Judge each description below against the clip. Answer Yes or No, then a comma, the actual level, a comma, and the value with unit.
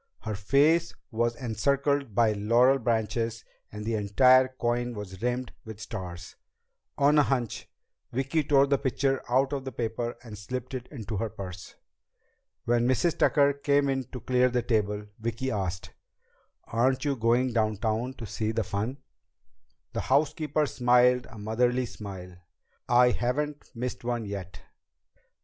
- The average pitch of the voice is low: Yes, low, 120 Hz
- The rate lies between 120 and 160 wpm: Yes, average, 145 wpm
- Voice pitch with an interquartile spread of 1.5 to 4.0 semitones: Yes, average, 3.3 semitones